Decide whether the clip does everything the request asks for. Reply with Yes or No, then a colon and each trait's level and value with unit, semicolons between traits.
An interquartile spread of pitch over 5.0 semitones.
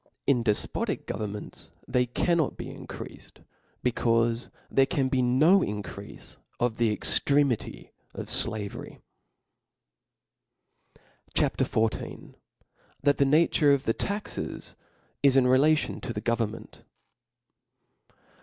No: average, 3.8 semitones